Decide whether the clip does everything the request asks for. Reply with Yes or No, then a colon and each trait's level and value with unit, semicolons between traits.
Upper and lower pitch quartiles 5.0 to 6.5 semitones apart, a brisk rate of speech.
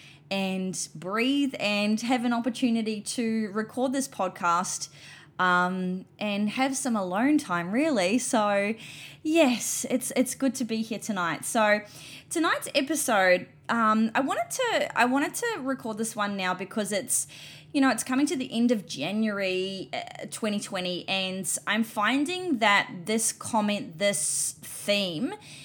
No: wide, 5.6 semitones; average, 140 wpm